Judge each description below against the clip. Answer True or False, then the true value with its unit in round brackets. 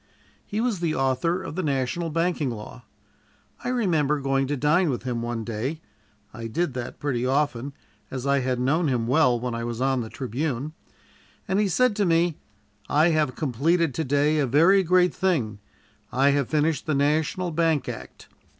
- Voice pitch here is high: False (145 Hz)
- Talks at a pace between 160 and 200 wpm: True (180 wpm)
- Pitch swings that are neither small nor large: True (4.7 semitones)